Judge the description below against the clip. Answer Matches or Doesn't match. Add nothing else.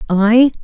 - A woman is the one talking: Matches